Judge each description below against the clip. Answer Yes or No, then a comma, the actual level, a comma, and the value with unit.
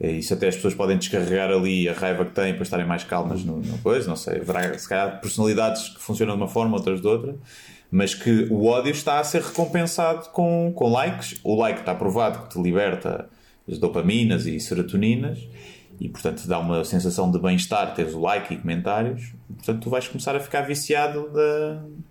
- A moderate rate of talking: No, fast, 210 wpm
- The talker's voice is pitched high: No, low, 105 Hz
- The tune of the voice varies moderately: No, wide, 8.2 semitones